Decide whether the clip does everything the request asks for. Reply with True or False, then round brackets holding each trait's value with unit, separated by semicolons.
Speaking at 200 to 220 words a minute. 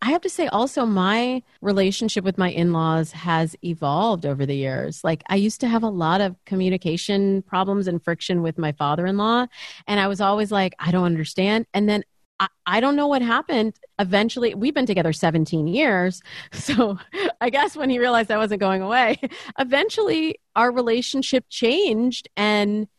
False (175 wpm)